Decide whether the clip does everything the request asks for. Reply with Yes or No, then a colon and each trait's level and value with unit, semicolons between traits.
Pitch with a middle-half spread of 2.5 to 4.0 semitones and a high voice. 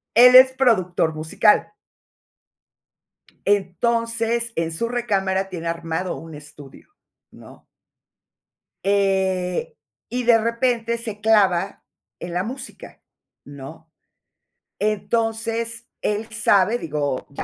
No: average, 5.1 semitones; high, 205 Hz